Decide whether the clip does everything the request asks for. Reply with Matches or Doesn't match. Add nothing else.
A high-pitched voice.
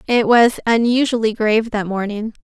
Matches